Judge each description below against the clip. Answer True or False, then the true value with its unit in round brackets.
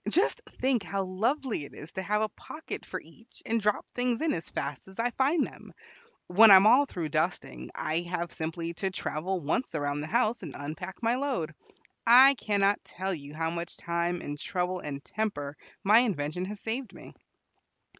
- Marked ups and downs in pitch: True (5.9 semitones)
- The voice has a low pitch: False (190 Hz)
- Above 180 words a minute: True (190 wpm)